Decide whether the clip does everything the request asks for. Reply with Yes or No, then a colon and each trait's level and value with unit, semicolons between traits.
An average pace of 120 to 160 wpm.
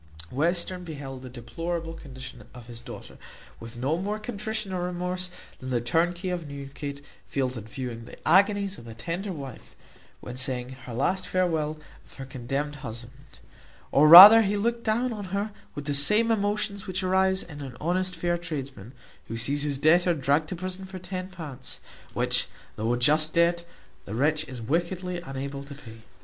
No: average, 175 wpm